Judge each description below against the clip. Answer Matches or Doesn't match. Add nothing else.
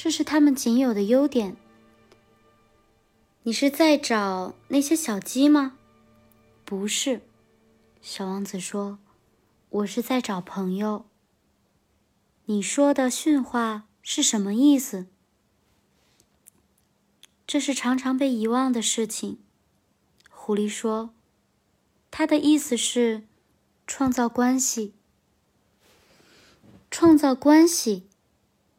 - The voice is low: Doesn't match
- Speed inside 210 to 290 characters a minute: Doesn't match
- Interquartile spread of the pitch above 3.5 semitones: Matches